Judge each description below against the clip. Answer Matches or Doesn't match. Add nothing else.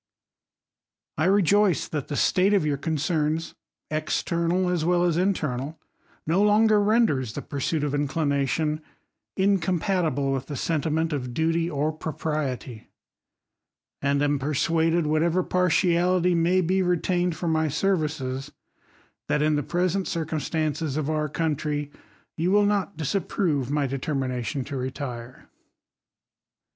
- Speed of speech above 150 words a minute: Doesn't match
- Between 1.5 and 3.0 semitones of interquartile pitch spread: Doesn't match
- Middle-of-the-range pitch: Matches